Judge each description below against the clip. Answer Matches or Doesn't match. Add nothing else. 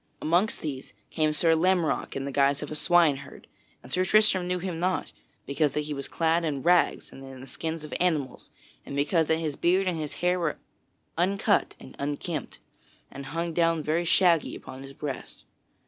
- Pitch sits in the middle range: Matches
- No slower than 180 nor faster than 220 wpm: Matches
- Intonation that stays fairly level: Doesn't match